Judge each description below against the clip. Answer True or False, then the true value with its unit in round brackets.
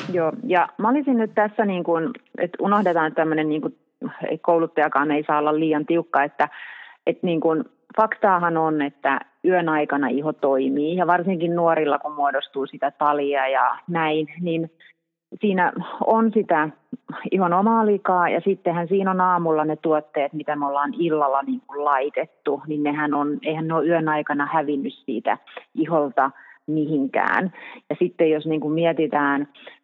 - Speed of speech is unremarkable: False (160 wpm)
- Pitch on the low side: False (160 Hz)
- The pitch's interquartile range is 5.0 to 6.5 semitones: False (3.2 semitones)